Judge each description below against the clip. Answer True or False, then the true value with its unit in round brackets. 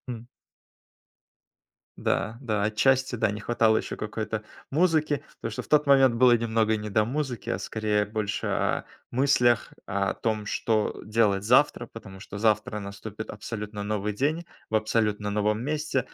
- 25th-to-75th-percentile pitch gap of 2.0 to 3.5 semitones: True (2.8 semitones)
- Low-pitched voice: True (110 Hz)